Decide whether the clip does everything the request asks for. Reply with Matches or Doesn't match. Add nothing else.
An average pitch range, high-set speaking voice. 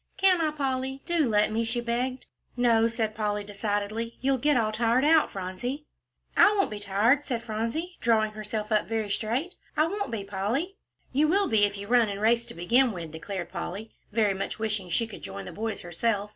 Matches